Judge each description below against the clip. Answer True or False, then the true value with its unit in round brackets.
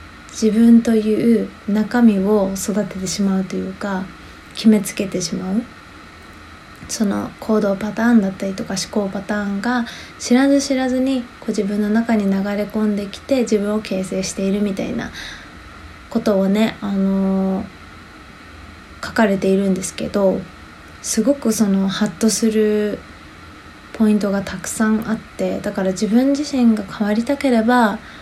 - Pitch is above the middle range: True (210 Hz)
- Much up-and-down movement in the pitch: False (2.6 semitones)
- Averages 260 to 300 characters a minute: True (290 characters per minute)